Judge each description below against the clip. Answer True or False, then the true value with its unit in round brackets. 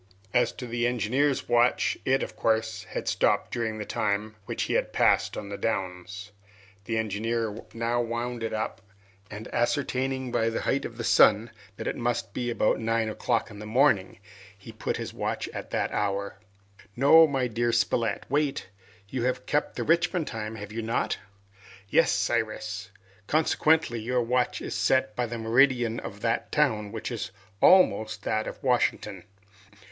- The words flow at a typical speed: True (170 wpm)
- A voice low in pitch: True (115 Hz)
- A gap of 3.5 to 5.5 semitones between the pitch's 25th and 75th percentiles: False (2.5 semitones)